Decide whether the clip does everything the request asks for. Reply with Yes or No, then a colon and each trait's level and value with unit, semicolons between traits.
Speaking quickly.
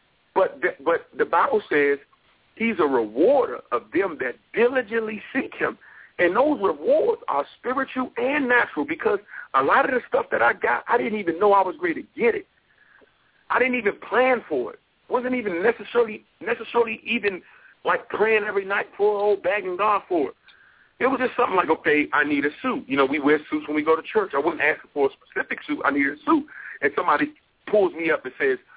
Yes: fast, 210 wpm